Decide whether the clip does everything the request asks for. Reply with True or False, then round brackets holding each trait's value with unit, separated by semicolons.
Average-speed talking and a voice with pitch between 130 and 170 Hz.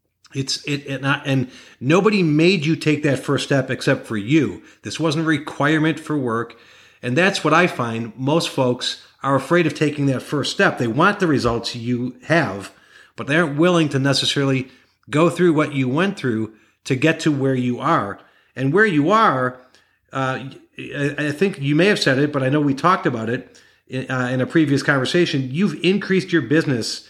True (195 wpm; 140 Hz)